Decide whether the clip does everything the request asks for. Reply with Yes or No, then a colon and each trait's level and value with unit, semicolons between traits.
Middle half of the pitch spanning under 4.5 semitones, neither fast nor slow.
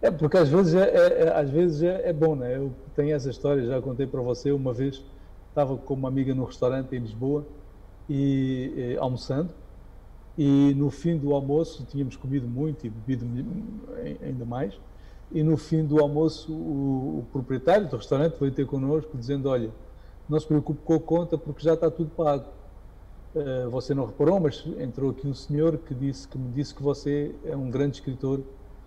Yes: average, 3.2 semitones; average, 190 wpm